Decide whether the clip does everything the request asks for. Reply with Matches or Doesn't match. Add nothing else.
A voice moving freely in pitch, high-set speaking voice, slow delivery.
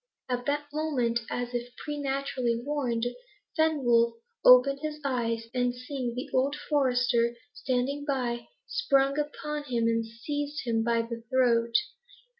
Doesn't match